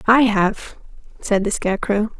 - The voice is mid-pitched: No, high, 210 Hz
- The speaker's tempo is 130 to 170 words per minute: Yes, slow, 135 wpm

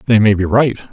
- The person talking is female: No, male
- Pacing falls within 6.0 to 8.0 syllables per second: Yes, 6.4 syllables/s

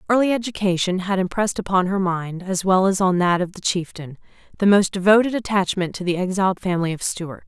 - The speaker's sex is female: Yes, female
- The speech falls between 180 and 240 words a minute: Yes, average, 200 wpm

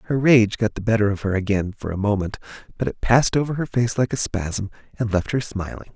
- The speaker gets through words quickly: Yes, fast, 240 wpm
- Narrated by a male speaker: Yes, male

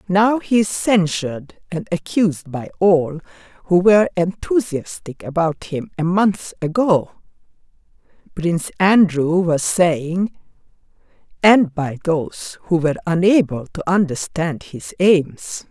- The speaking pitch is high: No, medium, 175 Hz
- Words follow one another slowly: Yes, slow, 115 wpm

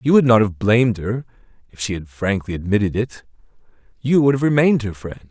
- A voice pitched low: Yes, low, 110 Hz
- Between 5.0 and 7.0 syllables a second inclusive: Yes, 5.9 syllables/s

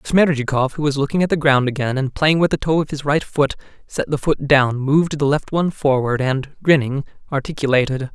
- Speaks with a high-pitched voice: No, medium, 140 Hz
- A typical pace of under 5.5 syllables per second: No, 5.6 syllables/s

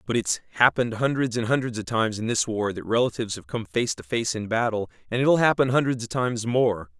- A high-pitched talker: No, low, 115 Hz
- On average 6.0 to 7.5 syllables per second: Yes, 6.1 syllables/s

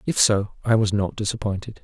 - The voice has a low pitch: Yes, low, 105 Hz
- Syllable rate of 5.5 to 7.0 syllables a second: Yes, 5.7 syllables/s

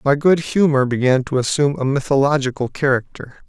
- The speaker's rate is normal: Yes, average, 155 wpm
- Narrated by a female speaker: No, male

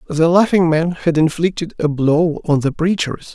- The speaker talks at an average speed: Yes, average, 180 wpm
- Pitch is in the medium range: Yes, medium, 165 Hz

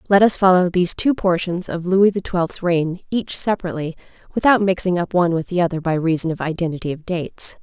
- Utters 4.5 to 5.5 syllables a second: No, 6.1 syllables/s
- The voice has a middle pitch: Yes, medium, 180 Hz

